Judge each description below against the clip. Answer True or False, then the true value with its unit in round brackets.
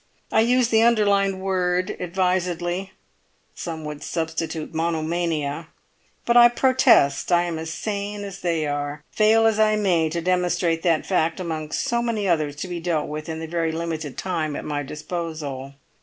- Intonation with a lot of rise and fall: False (3.6 semitones)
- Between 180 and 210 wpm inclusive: False (165 wpm)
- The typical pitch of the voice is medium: True (170 Hz)